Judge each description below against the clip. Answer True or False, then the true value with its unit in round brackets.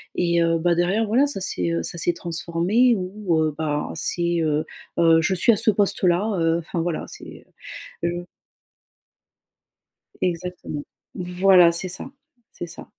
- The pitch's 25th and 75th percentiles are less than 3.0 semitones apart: True (2.5 semitones)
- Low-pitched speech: False (175 Hz)